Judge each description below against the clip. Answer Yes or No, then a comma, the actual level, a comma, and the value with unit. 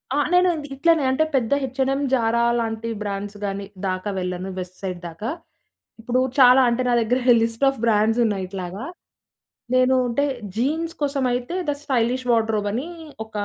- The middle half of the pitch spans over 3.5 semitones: Yes, average, 4.3 semitones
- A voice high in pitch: Yes, high, 235 Hz